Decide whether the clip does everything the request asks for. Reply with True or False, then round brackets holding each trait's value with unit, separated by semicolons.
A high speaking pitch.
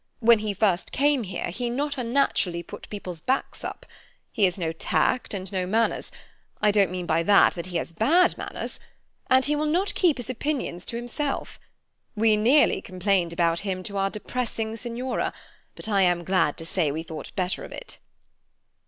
True (205 Hz)